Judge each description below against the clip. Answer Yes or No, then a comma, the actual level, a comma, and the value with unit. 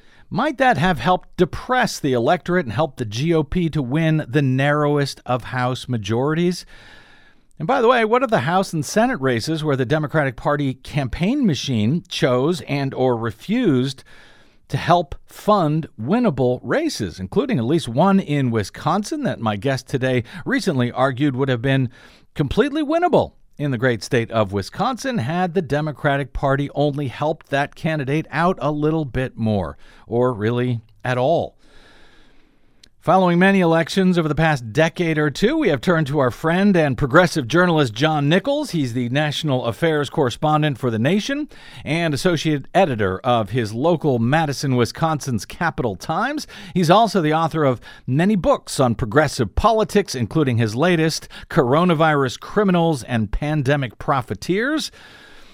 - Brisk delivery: No, average, 150 wpm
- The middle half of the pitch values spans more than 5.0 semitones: Yes, wide, 5.5 semitones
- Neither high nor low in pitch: Yes, medium, 150 Hz